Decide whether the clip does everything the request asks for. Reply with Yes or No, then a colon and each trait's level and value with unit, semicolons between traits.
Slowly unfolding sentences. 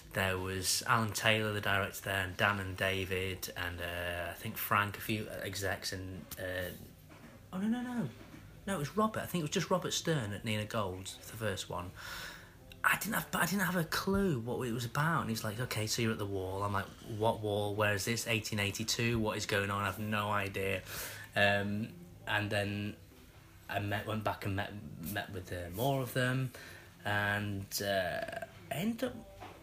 No: average, 200 wpm